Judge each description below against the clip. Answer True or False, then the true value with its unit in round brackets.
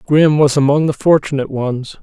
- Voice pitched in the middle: True (145 Hz)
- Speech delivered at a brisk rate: False (180 wpm)